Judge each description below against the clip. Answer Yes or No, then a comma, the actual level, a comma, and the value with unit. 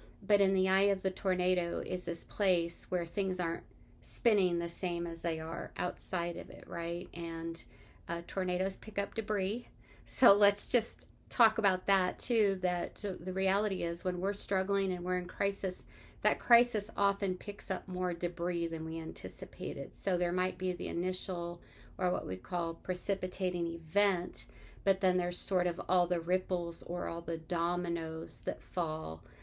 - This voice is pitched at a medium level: Yes, medium, 180 Hz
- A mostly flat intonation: Yes, narrow, 2.3 semitones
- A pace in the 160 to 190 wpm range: Yes, average, 170 wpm